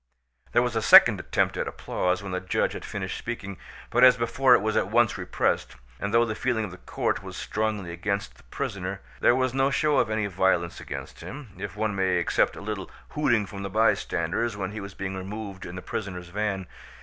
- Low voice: Yes, low, 105 Hz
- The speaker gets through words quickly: Yes, fast, 215 wpm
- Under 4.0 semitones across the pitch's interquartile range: Yes, average, 3.5 semitones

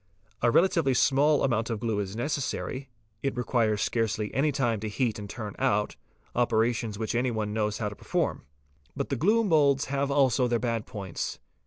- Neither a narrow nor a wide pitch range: Yes, average, 4.0 semitones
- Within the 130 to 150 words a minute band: No, average, 180 wpm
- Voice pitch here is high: No, low, 120 Hz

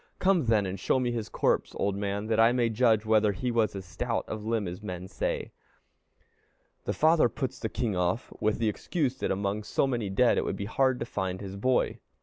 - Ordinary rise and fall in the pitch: Yes, average, 3.6 semitones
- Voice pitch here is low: Yes, low, 110 Hz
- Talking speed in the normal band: No, fast, 220 wpm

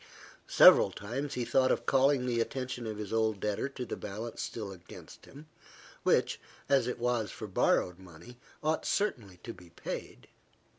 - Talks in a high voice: No, low, 115 Hz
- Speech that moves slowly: No, average, 165 wpm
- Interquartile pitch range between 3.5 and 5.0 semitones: Yes, average, 3.9 semitones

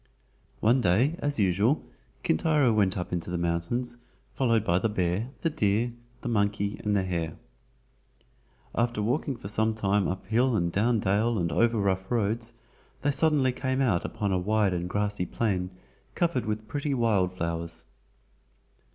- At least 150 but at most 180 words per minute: Yes, average, 160 wpm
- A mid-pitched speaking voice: No, low, 105 Hz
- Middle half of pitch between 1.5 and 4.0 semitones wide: No, average, 4.5 semitones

